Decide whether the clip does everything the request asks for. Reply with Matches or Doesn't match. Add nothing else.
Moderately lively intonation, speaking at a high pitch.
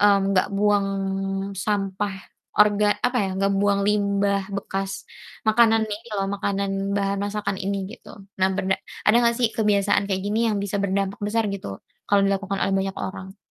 Doesn't match